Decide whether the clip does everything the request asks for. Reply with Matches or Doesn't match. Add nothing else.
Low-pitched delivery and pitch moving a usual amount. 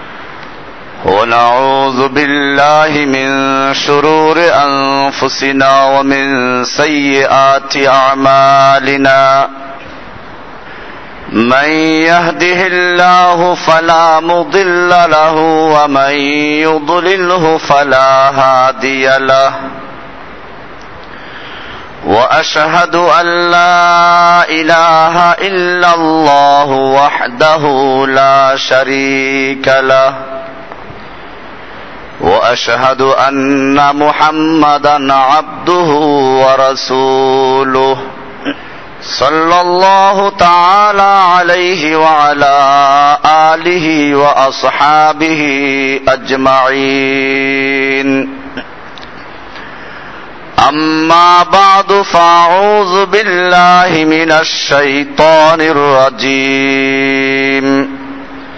Doesn't match